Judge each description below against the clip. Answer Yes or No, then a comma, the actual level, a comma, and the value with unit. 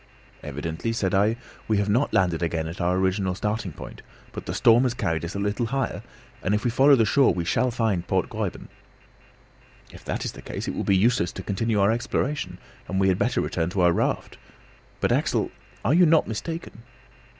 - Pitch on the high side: No, low, 100 Hz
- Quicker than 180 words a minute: Yes, fast, 205 wpm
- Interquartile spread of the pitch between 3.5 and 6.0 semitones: Yes, average, 4.6 semitones